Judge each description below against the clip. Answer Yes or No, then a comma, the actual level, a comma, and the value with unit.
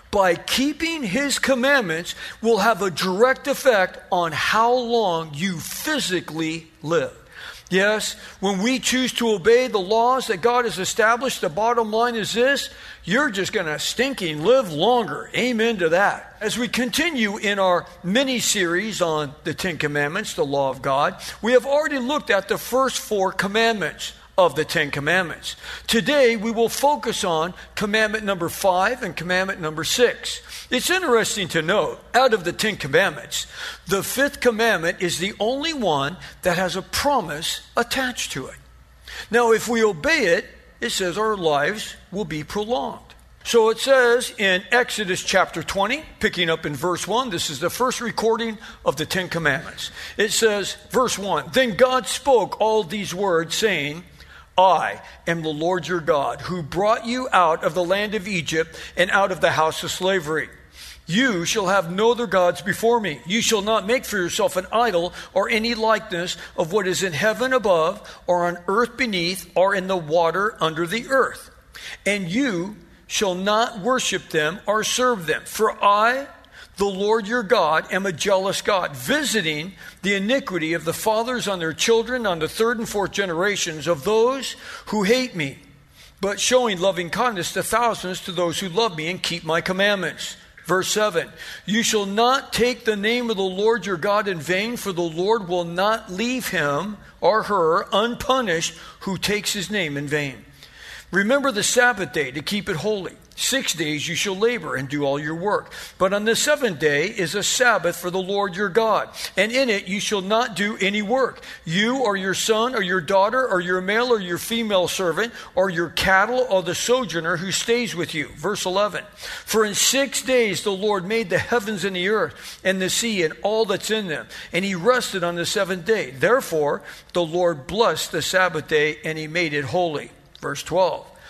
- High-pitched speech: Yes, high, 200 Hz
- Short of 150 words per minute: No, average, 180 wpm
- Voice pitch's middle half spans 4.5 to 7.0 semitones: Yes, average, 4.8 semitones